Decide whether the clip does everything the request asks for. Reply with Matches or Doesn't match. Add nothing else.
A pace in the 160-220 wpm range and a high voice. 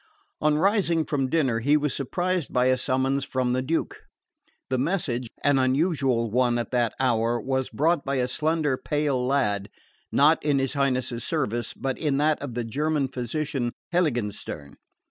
Doesn't match